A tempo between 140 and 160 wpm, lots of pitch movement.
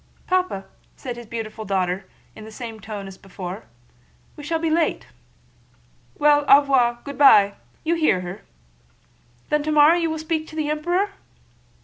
Yes: average, 155 wpm; wide, 6.9 semitones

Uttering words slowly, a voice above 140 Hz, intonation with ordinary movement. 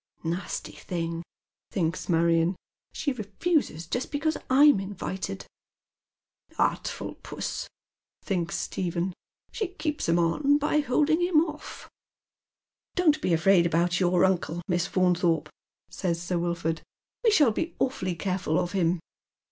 No: slow, 130 wpm; medium, 185 Hz; wide, 9.0 semitones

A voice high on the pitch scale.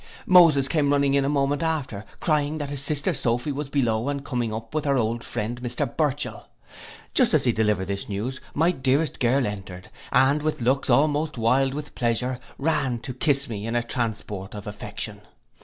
No: low, 135 Hz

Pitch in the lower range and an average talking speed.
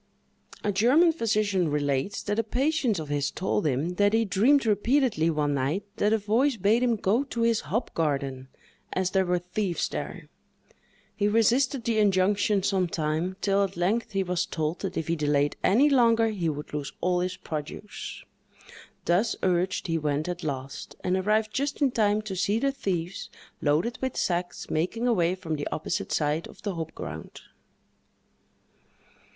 No: high, 190 Hz; average, 170 wpm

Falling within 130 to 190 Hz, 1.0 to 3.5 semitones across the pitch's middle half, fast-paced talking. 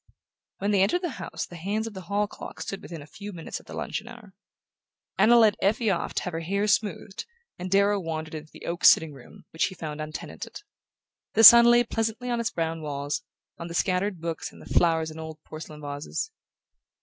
No: medium, 185 Hz; average, 4.7 semitones; fast, 210 wpm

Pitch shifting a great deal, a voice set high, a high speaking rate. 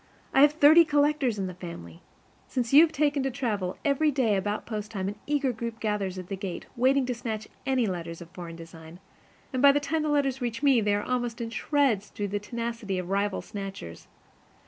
Yes: wide, 5.8 semitones; high, 230 Hz; fast, 215 wpm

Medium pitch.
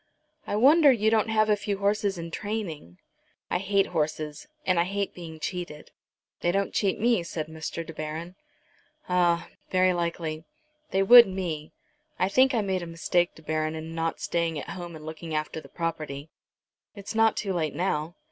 Yes: medium, 175 Hz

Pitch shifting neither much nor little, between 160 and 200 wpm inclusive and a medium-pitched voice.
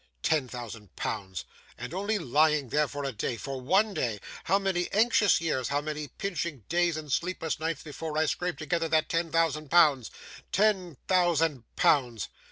Yes: average, 4.3 semitones; average, 170 wpm; medium, 155 Hz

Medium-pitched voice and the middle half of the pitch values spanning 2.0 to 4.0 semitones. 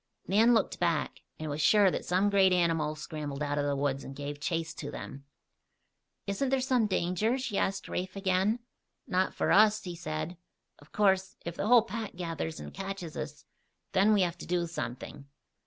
No: medium, 180 Hz; average, 4.7 semitones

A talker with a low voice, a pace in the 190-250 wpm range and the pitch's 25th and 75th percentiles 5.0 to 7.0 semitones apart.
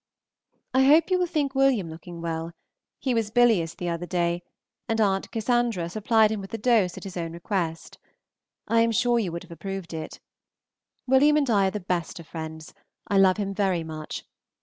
No: high, 195 Hz; average, 195 wpm; average, 5.3 semitones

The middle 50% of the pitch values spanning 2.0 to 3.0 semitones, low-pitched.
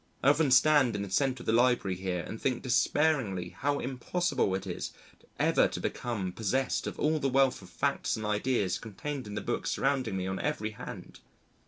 No: average, 5.3 semitones; low, 120 Hz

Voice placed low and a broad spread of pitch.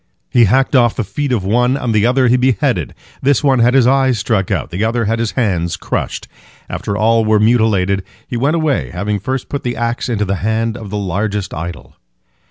No: low, 115 Hz; average, 3.7 semitones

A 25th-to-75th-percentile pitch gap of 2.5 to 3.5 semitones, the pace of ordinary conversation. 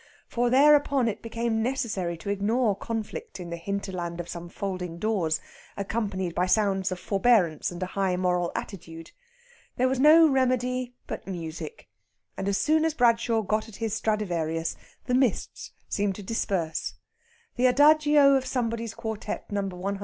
No: average, 5.2 semitones; average, 155 wpm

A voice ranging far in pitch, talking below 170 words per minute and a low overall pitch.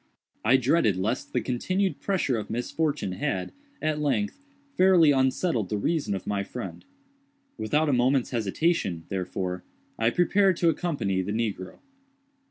Yes: wide, 8.2 semitones; average, 140 wpm; low, 125 Hz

